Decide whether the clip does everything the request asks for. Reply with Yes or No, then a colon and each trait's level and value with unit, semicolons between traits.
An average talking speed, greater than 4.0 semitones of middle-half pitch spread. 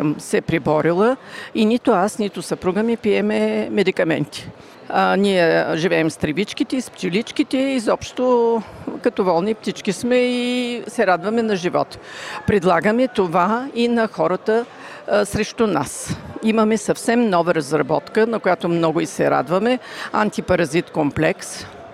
Yes: average, 130 wpm; average, 4.7 semitones